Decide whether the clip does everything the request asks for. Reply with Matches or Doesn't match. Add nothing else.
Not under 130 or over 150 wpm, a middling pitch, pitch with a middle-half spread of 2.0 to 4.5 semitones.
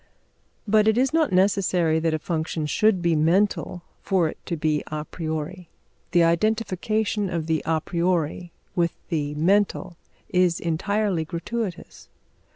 Matches